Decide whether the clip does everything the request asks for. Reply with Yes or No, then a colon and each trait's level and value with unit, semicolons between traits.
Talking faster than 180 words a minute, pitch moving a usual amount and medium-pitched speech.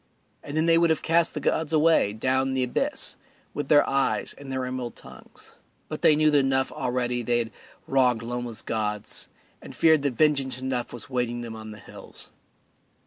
No: average, 190 wpm; average, 3.4 semitones; low, 130 Hz